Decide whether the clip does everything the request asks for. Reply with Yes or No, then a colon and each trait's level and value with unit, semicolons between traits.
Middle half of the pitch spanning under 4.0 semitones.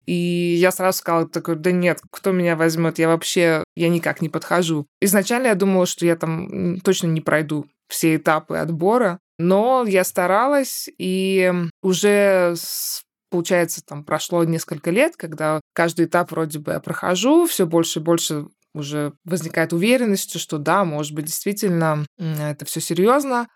Yes: narrow, 2.6 semitones